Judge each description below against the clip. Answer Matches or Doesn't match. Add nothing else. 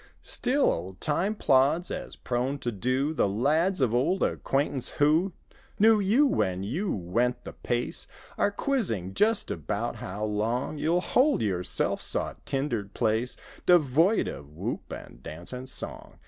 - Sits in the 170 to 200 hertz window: Doesn't match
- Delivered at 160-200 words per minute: Doesn't match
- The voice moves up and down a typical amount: Doesn't match